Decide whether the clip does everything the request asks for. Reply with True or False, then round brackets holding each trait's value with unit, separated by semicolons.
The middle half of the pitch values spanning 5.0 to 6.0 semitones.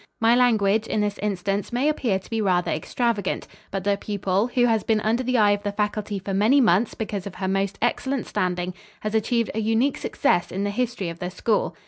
False (3.0 semitones)